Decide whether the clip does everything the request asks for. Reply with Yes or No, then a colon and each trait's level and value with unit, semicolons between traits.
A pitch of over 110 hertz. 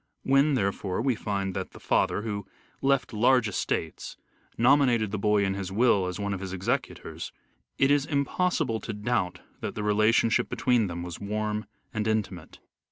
No: low, 105 Hz